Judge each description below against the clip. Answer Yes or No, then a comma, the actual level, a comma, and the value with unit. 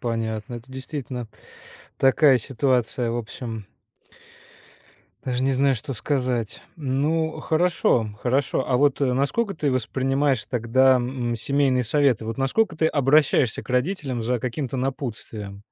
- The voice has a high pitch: No, low, 130 Hz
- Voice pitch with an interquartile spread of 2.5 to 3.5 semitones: Yes, average, 2.8 semitones